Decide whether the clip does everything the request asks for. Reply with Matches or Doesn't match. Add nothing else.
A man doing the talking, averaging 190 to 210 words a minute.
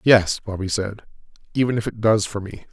Matches